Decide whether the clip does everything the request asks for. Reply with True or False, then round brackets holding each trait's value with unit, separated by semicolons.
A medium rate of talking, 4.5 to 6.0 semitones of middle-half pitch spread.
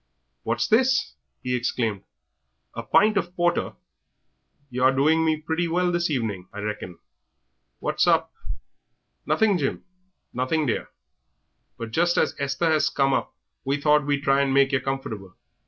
True (150 wpm; 4.9 semitones)